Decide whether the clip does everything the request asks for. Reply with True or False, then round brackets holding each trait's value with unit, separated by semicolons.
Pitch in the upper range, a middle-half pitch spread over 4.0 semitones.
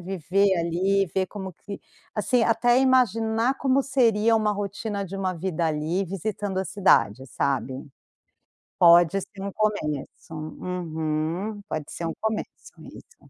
True (195 Hz; 4.4 semitones)